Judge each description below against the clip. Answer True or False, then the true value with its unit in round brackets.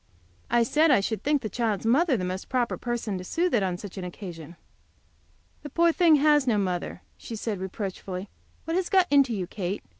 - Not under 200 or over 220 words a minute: True (205 wpm)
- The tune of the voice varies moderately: False (7.4 semitones)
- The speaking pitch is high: True (225 Hz)